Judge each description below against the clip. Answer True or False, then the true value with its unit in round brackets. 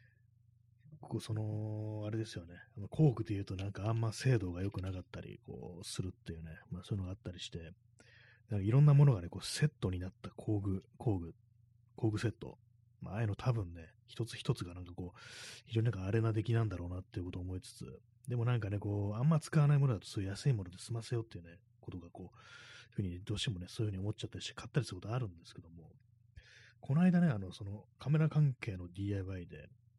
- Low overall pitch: True (110 Hz)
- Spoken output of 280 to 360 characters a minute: False (420 characters per minute)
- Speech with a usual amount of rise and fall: True (3.9 semitones)